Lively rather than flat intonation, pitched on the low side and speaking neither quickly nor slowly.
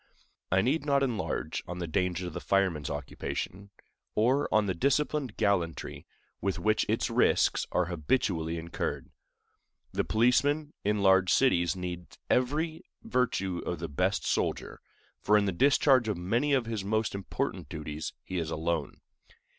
Yes: wide, 6.2 semitones; low, 100 Hz; average, 150 wpm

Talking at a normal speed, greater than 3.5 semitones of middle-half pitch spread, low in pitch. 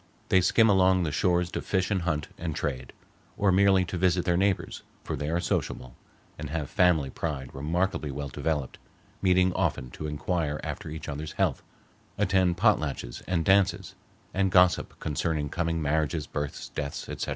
Yes: average, 165 wpm; average, 3.9 semitones; very low, 85 Hz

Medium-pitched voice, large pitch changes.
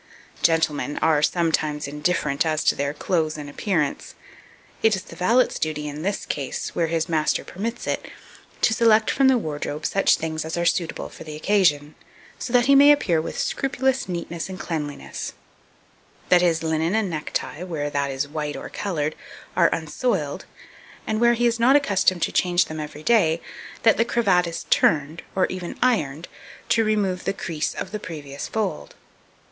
Yes: medium, 170 Hz; wide, 5.7 semitones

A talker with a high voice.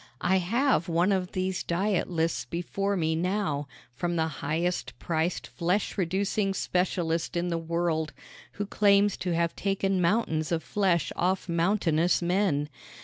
No: medium, 175 Hz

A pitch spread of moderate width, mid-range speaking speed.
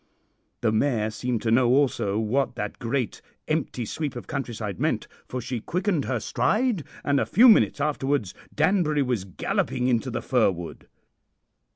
Yes: average, 4.5 semitones; average, 160 wpm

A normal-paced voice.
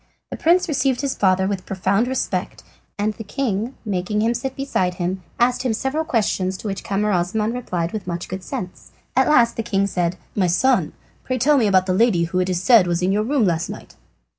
No: fast, 215 wpm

